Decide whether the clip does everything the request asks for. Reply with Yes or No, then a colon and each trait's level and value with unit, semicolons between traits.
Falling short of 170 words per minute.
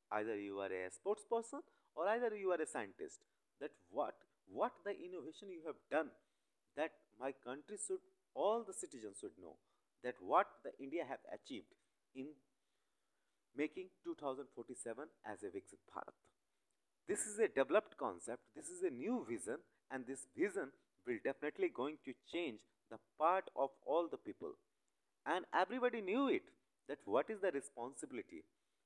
Yes: average, 155 wpm